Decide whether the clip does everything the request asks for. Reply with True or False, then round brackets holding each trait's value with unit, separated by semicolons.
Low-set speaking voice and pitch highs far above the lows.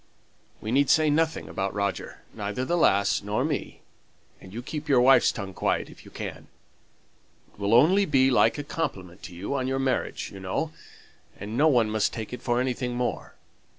True (125 Hz; 5.7 semitones)